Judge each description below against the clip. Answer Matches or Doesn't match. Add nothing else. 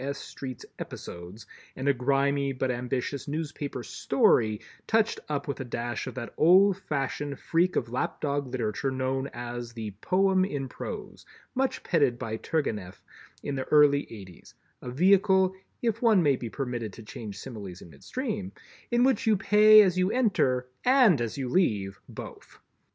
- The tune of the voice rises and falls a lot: Matches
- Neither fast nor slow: Matches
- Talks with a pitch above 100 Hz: Matches